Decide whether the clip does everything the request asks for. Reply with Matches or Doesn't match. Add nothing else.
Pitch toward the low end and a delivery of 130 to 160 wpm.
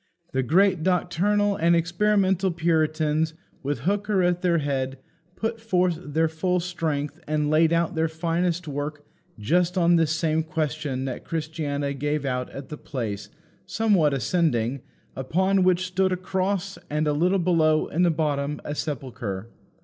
Doesn't match